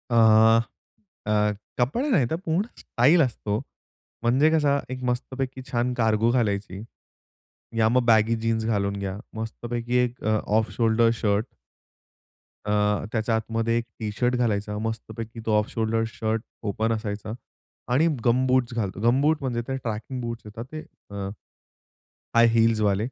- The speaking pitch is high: No, low, 115 Hz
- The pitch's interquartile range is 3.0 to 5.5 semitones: No, narrow, 2.4 semitones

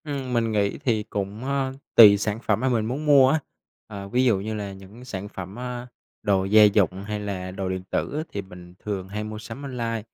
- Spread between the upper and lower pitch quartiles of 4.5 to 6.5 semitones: No, average, 3.9 semitones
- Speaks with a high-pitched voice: No, low, 105 Hz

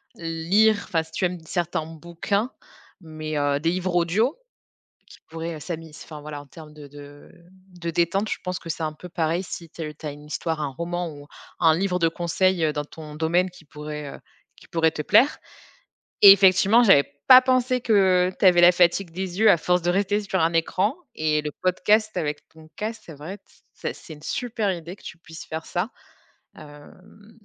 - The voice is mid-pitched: Yes, medium, 170 Hz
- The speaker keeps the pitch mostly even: No, average, 3.3 semitones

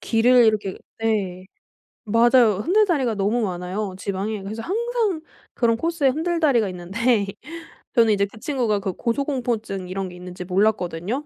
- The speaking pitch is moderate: No, high, 220 Hz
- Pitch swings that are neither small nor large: Yes, average, 4.7 semitones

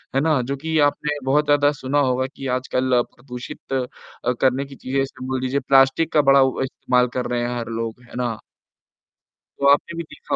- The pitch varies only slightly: Yes, narrow, 2.2 semitones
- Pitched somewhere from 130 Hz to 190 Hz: Yes, low, 135 Hz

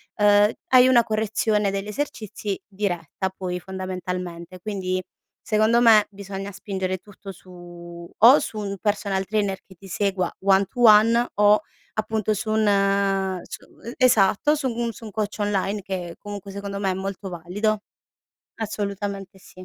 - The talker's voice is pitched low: No, high, 200 Hz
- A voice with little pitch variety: Yes, narrow, 2.2 semitones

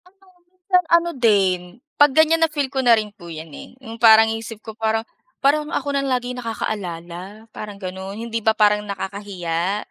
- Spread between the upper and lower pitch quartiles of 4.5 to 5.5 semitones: Yes, average, 5.2 semitones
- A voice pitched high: Yes, high, 220 Hz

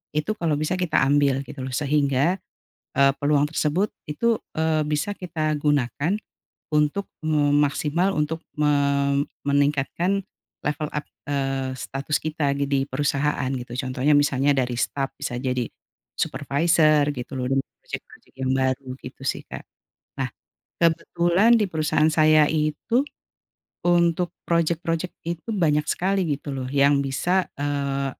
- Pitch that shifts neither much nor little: Yes, average, 3.1 semitones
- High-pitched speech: No, medium, 150 Hz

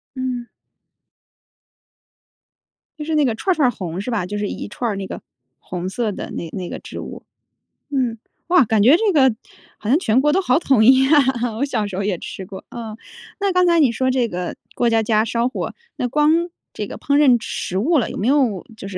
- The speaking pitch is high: Yes, high, 240 Hz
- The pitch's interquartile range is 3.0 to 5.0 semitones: No, wide, 5.5 semitones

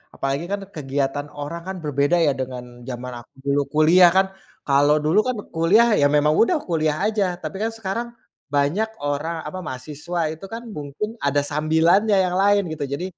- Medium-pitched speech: Yes, medium, 155 Hz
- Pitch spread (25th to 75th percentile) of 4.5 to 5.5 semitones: Yes, average, 5.0 semitones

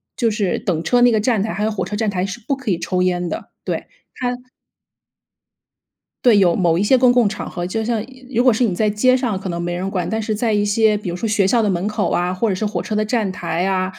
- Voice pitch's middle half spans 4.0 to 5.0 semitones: No, average, 3.5 semitones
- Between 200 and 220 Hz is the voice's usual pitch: Yes, high, 210 Hz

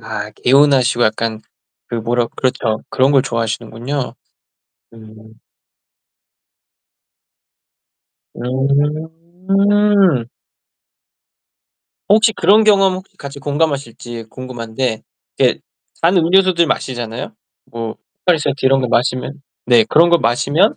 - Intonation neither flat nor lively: No, wide, 6.2 semitones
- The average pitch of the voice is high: No, low, 135 Hz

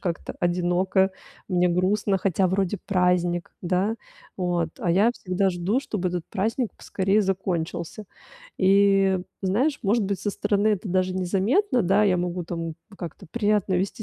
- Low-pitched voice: No, high, 190 Hz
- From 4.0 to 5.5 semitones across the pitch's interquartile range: No, narrow, 2.4 semitones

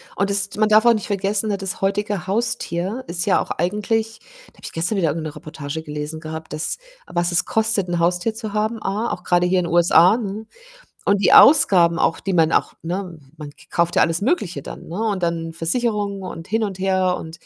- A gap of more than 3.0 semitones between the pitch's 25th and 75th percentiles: Yes, average, 3.8 semitones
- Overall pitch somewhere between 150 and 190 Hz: Yes, medium, 185 Hz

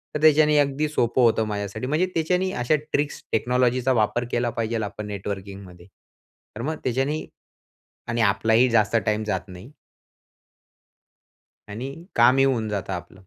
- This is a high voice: No, low, 120 Hz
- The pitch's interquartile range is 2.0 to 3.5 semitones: No, average, 4.3 semitones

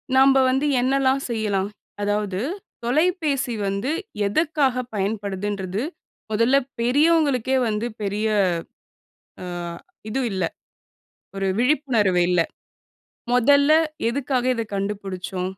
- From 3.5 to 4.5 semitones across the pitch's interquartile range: No, average, 5.2 semitones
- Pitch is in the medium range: No, high, 230 Hz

